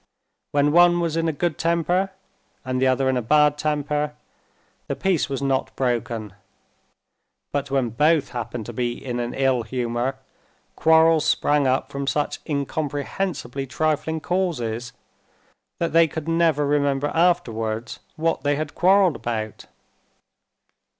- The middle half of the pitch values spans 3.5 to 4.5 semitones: Yes, average, 4.2 semitones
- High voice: No, medium, 145 Hz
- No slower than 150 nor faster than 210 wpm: No, slow, 135 wpm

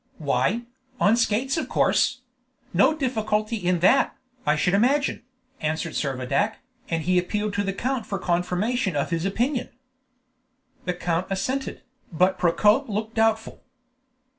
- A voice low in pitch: No, high, 205 Hz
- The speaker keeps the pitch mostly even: No, average, 5.0 semitones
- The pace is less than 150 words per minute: Yes, slow, 135 wpm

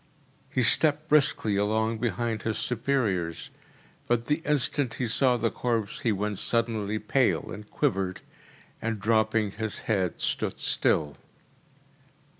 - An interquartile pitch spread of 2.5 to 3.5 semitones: Yes, average, 2.9 semitones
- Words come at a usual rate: No, slow, 125 wpm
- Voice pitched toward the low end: Yes, low, 110 Hz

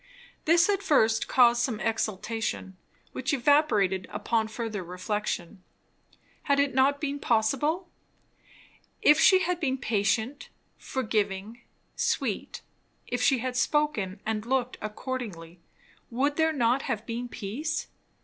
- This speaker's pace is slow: Yes, slow, 120 wpm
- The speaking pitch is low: No, high, 240 Hz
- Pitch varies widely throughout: No, average, 4.9 semitones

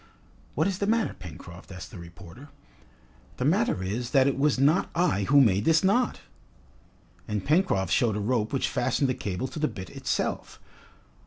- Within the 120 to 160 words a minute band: No, average, 175 wpm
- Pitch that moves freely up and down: Yes, wide, 8.2 semitones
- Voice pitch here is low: Yes, low, 130 Hz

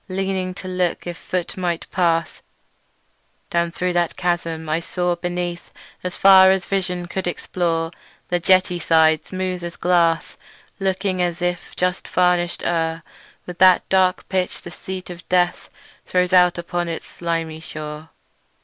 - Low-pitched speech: No, medium, 175 Hz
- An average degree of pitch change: No, narrow, 1.4 semitones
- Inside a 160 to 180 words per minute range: No, average, 150 wpm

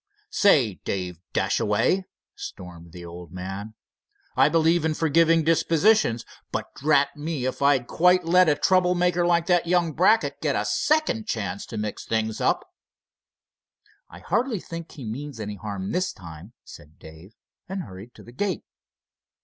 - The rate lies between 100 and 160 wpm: Yes, average, 155 wpm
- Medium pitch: Yes, medium, 150 Hz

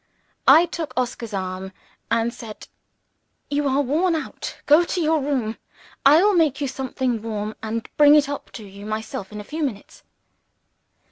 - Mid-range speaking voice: No, very high, 260 Hz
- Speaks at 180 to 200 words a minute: No, average, 165 wpm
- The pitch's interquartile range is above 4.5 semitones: Yes, wide, 5.5 semitones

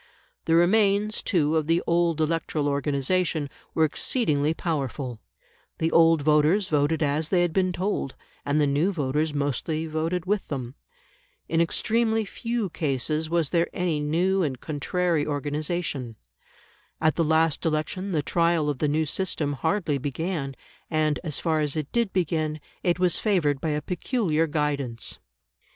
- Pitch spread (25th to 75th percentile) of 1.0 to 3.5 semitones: Yes, average, 3.1 semitones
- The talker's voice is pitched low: No, medium, 160 Hz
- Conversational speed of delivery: Yes, average, 150 wpm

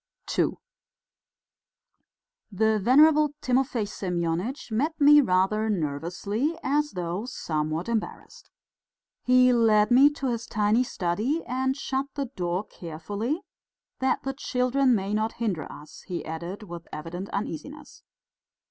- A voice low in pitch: No, high, 220 Hz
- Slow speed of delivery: Yes, slow, 120 wpm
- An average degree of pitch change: No, wide, 6.6 semitones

